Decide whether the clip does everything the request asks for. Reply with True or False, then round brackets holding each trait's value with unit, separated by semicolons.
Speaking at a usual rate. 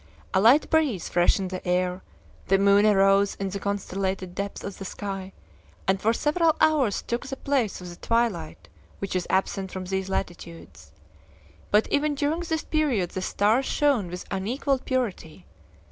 True (160 wpm)